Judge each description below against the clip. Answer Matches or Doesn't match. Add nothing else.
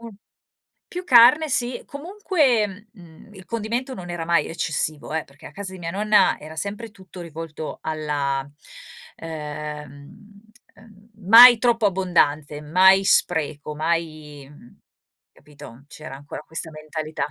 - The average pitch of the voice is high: Doesn't match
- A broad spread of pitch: Matches